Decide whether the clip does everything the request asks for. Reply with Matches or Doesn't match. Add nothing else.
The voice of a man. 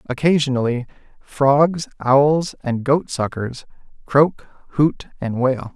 Matches